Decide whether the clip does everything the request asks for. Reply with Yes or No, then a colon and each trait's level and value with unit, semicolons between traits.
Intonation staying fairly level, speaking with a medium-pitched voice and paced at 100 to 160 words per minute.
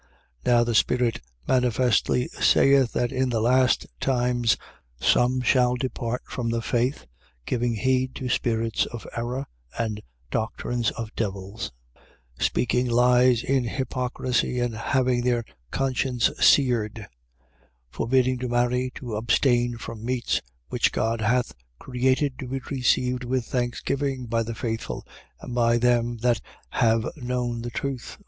No: narrow, 1.5 semitones; low, 120 Hz; average, 140 wpm